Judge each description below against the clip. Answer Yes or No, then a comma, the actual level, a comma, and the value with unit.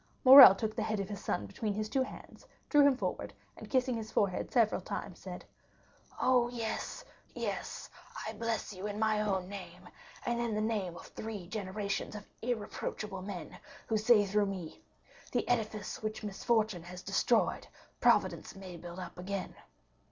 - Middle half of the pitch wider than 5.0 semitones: No, average, 2.9 semitones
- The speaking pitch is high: Yes, high, 210 Hz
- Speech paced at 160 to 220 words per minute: Yes, average, 165 wpm